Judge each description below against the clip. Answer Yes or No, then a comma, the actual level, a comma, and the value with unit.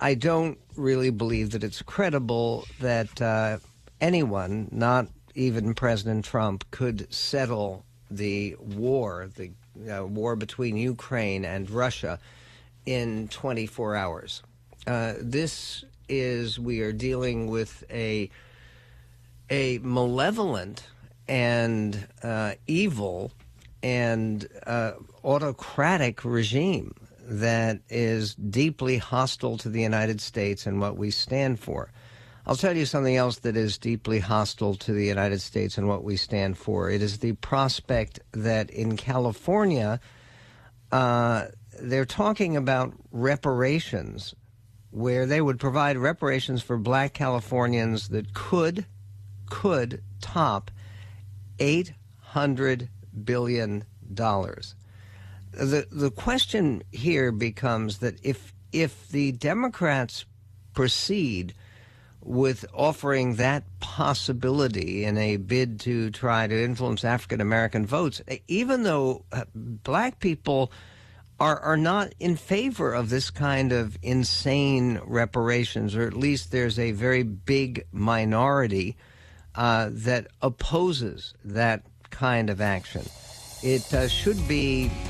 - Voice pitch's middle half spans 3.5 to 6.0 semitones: Yes, average, 3.8 semitones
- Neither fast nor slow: No, slow, 115 wpm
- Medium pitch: No, low, 115 Hz